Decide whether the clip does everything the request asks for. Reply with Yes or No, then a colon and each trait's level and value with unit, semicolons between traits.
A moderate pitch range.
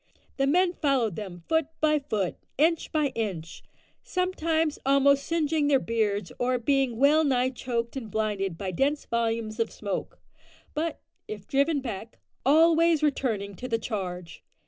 No: wide, 5.7 semitones